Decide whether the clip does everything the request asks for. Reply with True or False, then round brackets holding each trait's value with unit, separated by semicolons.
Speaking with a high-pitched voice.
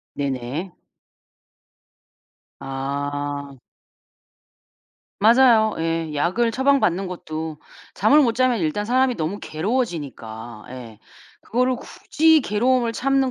False (180 Hz)